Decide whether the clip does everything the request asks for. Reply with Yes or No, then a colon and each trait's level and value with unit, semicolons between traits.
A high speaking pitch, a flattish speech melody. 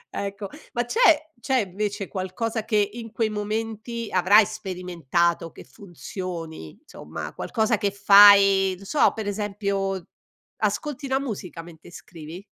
No: high, 200 Hz; average, 3.2 semitones